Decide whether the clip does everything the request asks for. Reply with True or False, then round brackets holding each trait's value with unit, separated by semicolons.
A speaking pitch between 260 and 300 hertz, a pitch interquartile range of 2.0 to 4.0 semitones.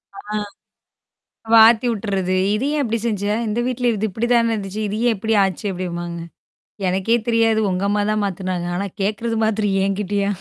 False (210 Hz; 2.8 semitones)